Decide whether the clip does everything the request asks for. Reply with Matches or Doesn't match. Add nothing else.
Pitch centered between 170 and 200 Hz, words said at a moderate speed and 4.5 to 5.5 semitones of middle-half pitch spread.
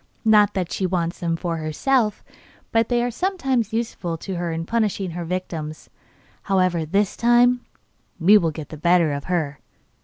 Matches